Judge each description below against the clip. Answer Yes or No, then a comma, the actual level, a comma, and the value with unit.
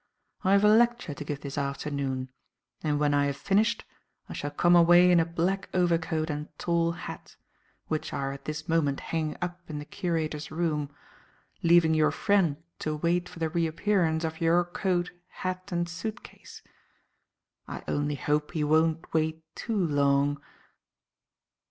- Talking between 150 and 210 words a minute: Yes, average, 160 wpm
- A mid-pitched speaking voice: Yes, medium, 160 Hz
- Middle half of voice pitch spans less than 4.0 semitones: Yes, average, 2.8 semitones